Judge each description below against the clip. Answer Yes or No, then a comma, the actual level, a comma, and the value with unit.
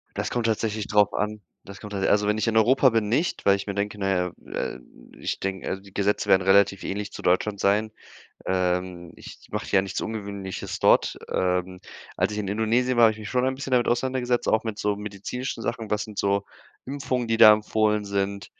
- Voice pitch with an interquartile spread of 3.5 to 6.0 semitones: No, narrow, 2.4 semitones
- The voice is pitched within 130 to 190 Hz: No, low, 105 Hz